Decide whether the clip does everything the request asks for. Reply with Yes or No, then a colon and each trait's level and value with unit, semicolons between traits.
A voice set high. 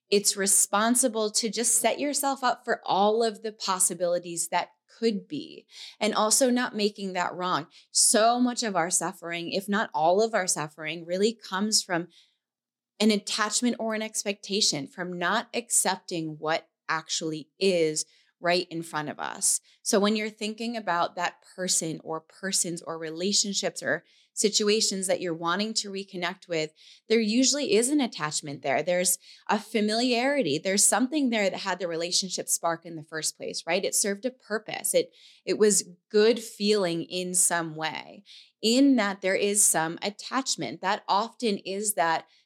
Yes: high, 200 Hz